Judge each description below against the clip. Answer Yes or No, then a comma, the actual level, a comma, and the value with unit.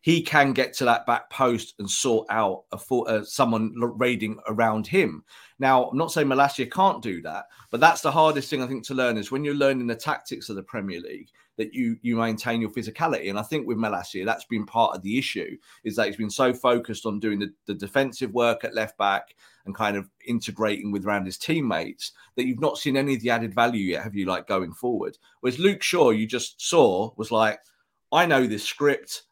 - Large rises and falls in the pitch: No, average, 3.7 semitones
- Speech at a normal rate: No, fast, 225 wpm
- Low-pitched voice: Yes, low, 120 Hz